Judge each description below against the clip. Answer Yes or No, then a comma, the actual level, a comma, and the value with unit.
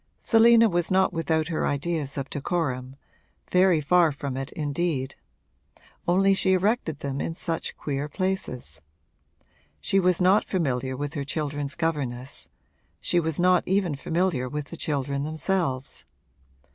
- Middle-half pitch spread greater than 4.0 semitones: Yes, average, 4.6 semitones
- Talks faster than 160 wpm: No, slow, 135 wpm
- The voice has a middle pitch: Yes, medium, 160 Hz